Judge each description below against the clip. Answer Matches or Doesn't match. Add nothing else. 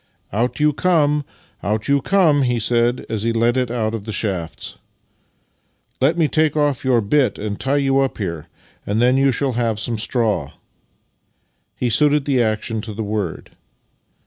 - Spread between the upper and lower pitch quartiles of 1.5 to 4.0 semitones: Doesn't match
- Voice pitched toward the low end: Matches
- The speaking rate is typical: Matches